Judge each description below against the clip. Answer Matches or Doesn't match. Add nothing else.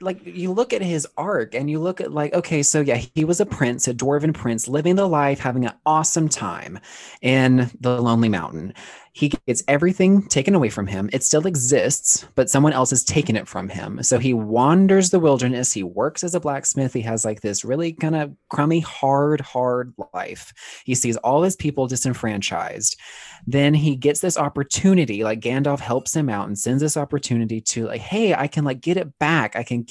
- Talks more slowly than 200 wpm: Doesn't match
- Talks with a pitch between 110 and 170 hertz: Matches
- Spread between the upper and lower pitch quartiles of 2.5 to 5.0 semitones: Matches